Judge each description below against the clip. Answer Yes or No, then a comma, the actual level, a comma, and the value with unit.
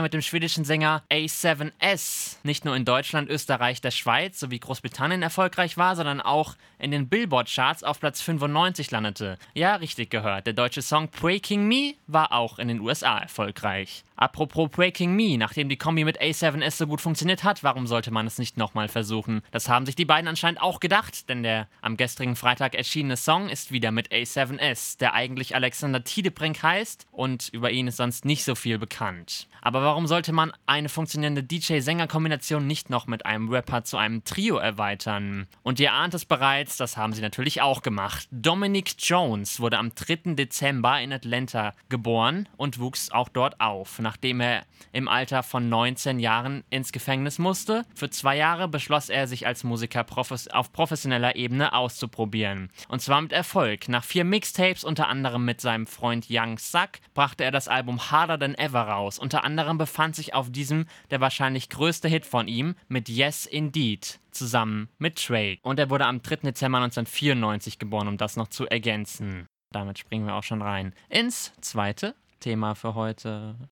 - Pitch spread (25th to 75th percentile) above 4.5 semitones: Yes, average, 5.1 semitones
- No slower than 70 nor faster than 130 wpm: No, average, 180 wpm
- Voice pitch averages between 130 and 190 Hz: Yes, low, 135 Hz